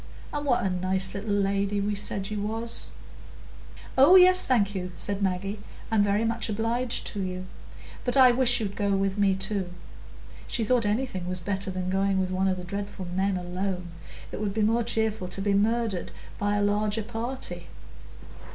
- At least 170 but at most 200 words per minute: Yes, average, 180 wpm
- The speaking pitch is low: No, high, 205 Hz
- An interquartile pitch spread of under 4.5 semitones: Yes, average, 2.8 semitones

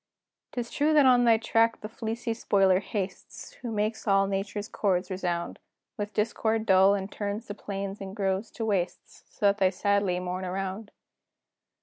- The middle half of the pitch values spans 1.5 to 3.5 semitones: Yes, narrow, 2.6 semitones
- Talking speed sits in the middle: Yes, average, 165 wpm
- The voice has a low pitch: No, high, 200 Hz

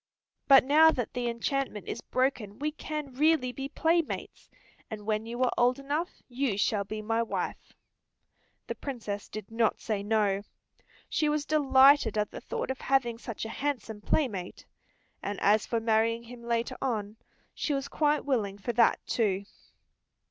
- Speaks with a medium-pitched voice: No, high, 235 Hz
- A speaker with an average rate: Yes, average, 165 wpm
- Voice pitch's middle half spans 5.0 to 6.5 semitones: No, average, 4.3 semitones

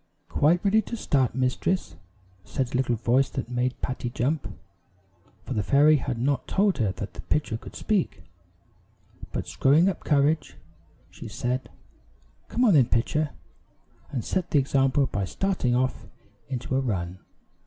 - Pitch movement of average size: Yes, average, 3.9 semitones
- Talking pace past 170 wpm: No, average, 155 wpm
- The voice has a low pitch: Yes, low, 130 Hz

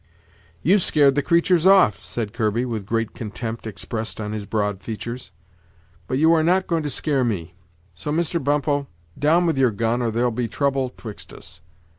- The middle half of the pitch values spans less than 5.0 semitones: No, wide, 5.5 semitones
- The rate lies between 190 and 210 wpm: No, average, 180 wpm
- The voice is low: Yes, low, 125 Hz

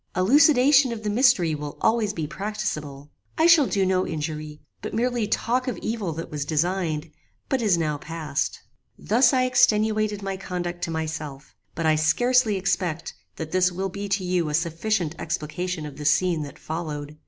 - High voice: No, medium, 180 Hz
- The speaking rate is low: No, average, 175 wpm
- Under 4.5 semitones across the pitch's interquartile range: No, wide, 5.6 semitones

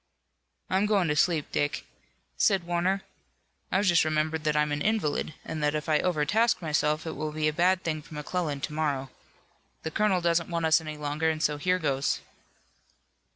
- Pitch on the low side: No, medium, 155 Hz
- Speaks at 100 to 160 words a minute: No, average, 185 wpm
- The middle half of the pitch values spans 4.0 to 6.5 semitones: No, average, 2.9 semitones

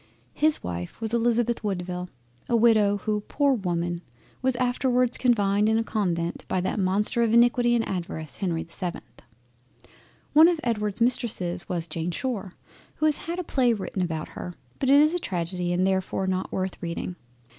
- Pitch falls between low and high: No, high, 205 Hz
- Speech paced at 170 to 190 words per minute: Yes, average, 175 wpm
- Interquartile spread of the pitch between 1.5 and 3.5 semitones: No, average, 5.1 semitones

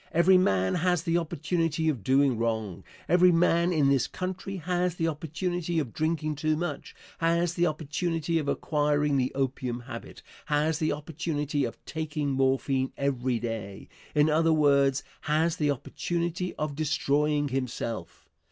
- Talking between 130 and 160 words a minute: Yes, average, 145 wpm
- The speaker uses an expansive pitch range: No, average, 3.5 semitones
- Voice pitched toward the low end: No, medium, 150 Hz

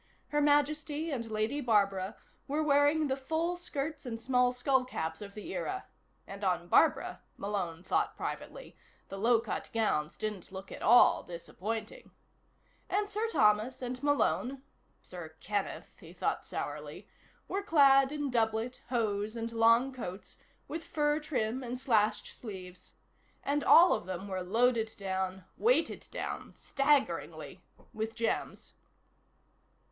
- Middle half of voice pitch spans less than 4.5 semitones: No, wide, 5.6 semitones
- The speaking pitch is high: Yes, high, 245 Hz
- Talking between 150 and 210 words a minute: No, slow, 135 wpm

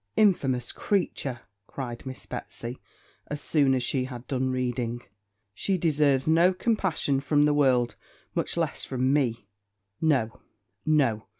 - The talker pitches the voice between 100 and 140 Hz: Yes, low, 135 Hz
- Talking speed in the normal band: No, slow, 130 wpm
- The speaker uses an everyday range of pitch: Yes, average, 3.5 semitones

